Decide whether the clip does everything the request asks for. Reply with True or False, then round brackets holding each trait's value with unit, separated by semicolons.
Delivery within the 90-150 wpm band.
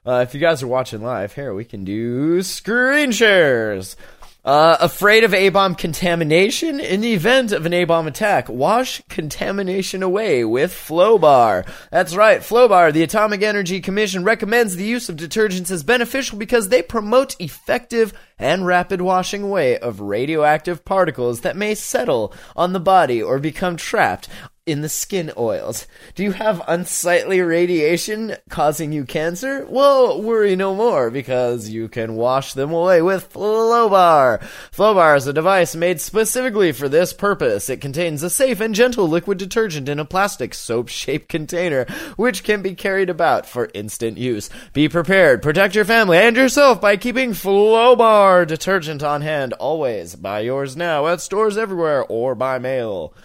False (160 wpm)